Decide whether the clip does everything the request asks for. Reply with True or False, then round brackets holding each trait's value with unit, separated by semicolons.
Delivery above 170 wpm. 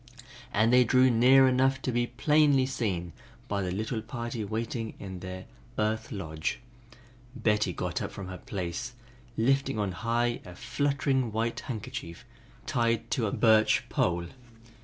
False (145 wpm)